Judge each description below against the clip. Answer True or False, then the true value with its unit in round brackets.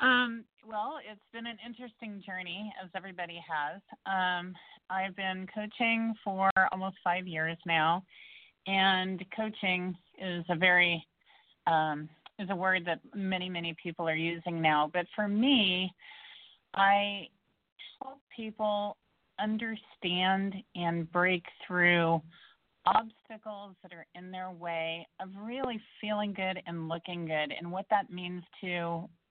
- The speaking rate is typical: False (130 wpm)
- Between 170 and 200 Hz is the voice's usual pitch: True (190 Hz)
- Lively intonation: False (3.2 semitones)